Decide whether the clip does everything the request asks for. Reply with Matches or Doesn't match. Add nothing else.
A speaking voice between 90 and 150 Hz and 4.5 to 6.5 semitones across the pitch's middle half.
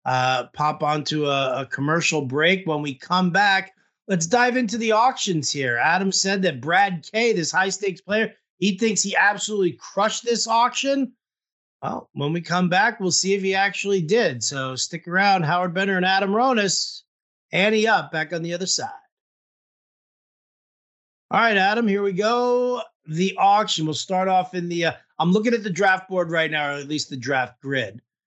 Doesn't match